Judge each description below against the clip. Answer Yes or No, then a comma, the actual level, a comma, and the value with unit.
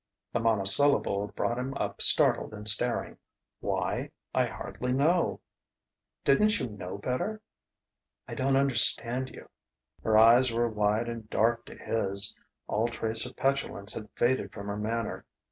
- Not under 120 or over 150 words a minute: Yes, average, 145 wpm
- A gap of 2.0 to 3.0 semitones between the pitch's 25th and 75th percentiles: No, average, 3.4 semitones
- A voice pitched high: No, low, 115 Hz